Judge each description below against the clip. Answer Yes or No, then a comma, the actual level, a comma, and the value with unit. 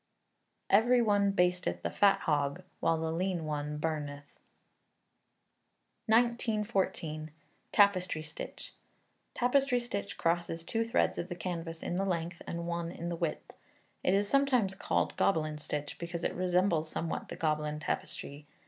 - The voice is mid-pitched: Yes, medium, 175 Hz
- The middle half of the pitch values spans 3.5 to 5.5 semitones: Yes, average, 4.2 semitones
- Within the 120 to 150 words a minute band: Yes, average, 140 wpm